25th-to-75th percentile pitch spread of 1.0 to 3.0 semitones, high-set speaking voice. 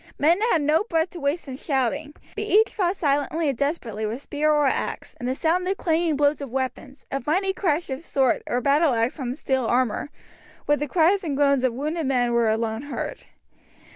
No: average, 3.9 semitones; very high, 285 Hz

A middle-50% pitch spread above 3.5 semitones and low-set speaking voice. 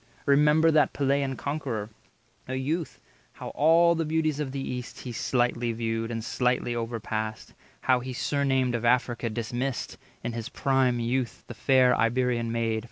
No: average, 3.0 semitones; low, 125 Hz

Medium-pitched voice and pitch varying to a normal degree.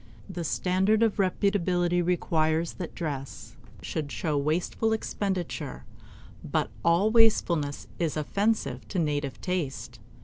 Yes: medium, 175 Hz; average, 4.0 semitones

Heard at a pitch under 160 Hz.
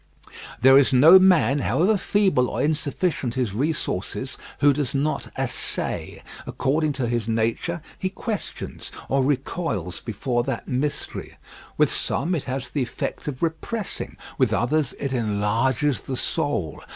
Yes: low, 135 Hz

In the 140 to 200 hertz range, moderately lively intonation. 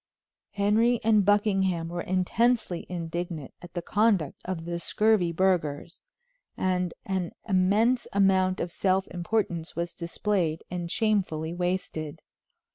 Yes: medium, 185 Hz; average, 3.0 semitones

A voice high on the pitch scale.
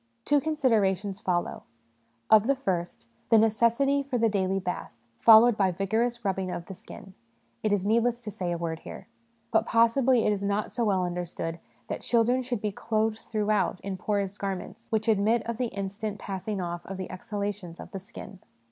Yes: high, 205 Hz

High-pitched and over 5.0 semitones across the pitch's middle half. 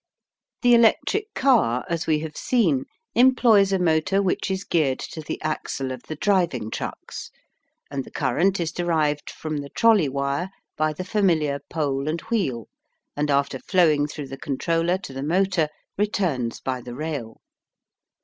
No: medium, 155 Hz; wide, 5.4 semitones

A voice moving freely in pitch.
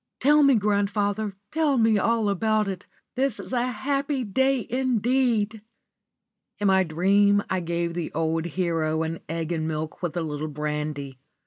Yes: wide, 6.1 semitones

